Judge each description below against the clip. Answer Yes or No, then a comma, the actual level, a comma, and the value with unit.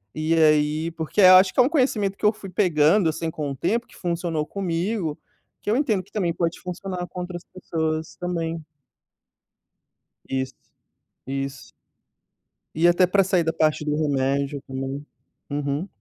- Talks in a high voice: No, medium, 165 Hz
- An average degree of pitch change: Yes, average, 3.6 semitones